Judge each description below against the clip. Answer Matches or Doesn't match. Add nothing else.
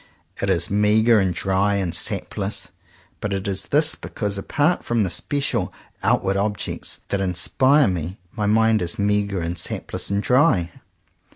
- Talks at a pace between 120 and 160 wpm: Matches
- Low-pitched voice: Matches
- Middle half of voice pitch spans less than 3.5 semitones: Matches